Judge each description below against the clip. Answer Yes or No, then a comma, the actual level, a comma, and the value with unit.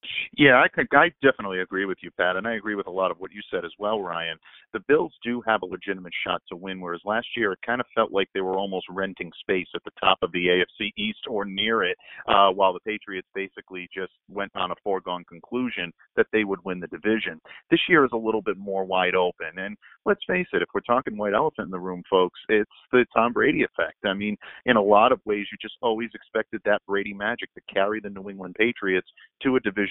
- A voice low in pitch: Yes, low, 100 Hz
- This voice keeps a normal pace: No, fast, 245 wpm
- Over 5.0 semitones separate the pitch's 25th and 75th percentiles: No, average, 2.8 semitones